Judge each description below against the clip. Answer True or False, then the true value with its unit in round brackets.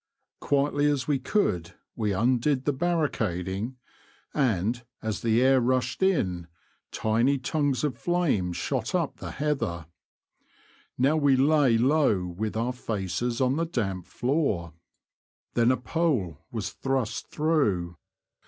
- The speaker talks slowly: True (125 wpm)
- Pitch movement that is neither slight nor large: False (5.8 semitones)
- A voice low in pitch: True (125 Hz)